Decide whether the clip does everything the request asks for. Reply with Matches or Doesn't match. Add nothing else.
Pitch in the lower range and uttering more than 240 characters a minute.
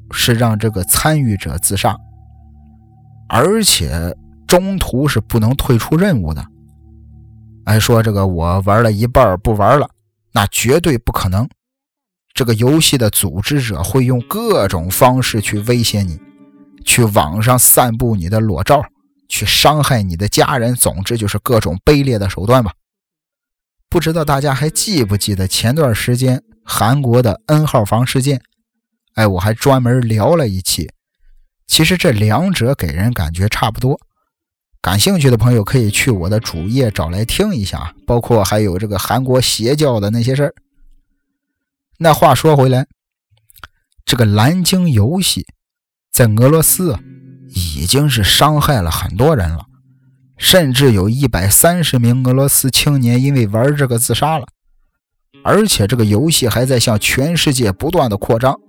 Doesn't match